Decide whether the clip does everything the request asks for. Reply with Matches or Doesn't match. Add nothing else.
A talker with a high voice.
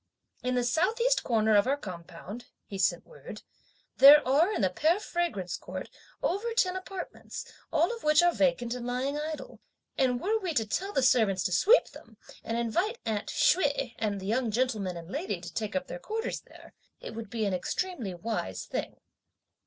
Matches